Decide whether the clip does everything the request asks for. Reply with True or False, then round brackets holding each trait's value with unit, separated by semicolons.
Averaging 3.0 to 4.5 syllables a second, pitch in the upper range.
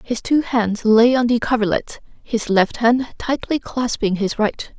True (4.2 syllables/s; 230 Hz)